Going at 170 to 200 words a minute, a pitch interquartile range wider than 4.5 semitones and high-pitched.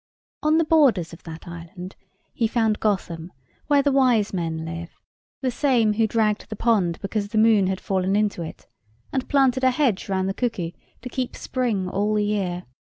Yes: average, 185 wpm; average, 5.1 semitones; high, 210 Hz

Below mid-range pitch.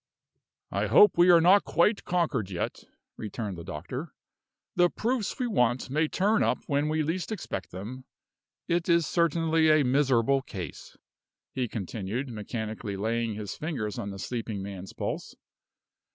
Yes: low, 130 Hz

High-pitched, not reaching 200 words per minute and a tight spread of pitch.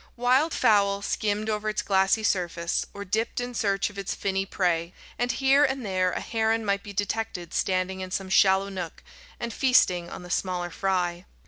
No: high, 200 Hz; average, 185 wpm; average, 3.2 semitones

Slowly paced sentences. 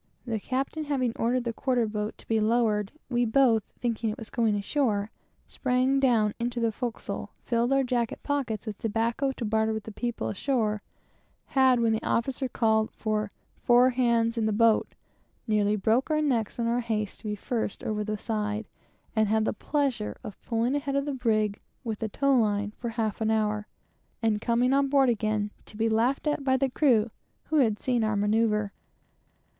No: average, 180 wpm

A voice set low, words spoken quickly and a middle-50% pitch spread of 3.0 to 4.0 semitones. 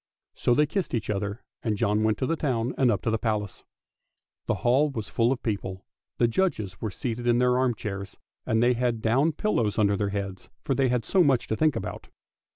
Yes: low, 115 Hz; fast, 220 wpm; average, 3.6 semitones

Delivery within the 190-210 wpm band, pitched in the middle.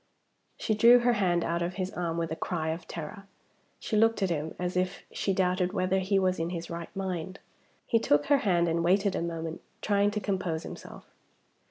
Yes: fast, 205 wpm; medium, 180 Hz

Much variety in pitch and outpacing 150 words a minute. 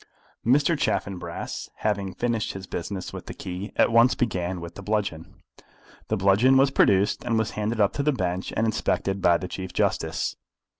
No: average, 3.7 semitones; average, 180 wpm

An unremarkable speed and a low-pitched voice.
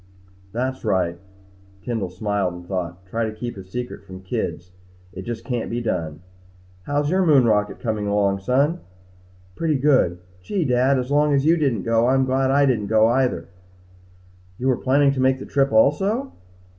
Yes: average, 180 wpm; low, 120 Hz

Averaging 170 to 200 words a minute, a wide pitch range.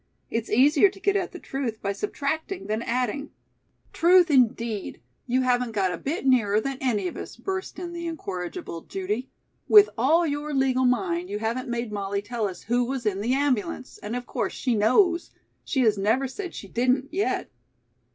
Yes: average, 190 wpm; wide, 5.7 semitones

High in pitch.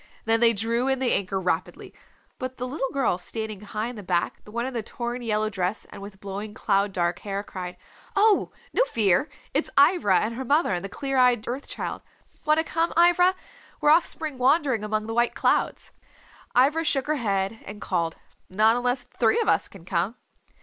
Yes: high, 230 Hz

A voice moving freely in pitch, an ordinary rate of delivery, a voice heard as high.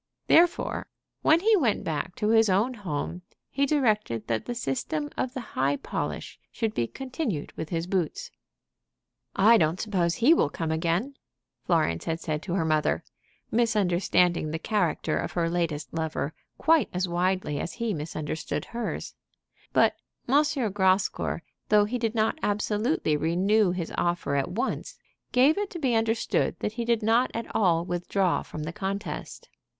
Yes: wide, 6.0 semitones; average, 160 wpm; high, 195 Hz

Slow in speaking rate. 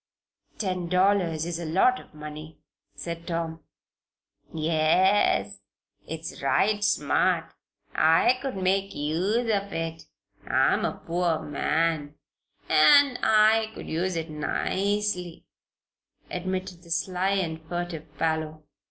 Yes: slow, 110 wpm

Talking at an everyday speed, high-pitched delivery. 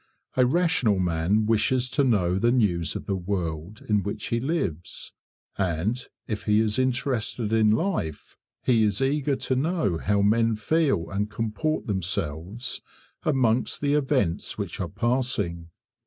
No: average, 145 wpm; low, 110 Hz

